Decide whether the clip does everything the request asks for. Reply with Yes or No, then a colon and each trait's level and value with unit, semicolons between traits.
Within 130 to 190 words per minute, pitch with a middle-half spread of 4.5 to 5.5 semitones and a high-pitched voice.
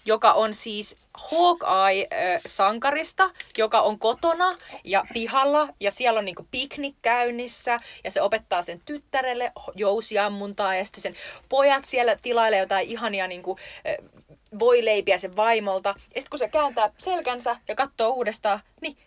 Yes: average, 140 wpm; average, 5.2 semitones; high, 230 Hz